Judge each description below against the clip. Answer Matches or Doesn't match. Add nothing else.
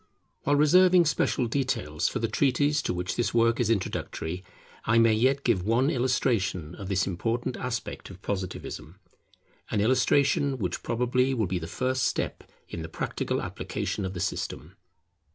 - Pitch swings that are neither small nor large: Doesn't match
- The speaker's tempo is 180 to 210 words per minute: Doesn't match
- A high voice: Doesn't match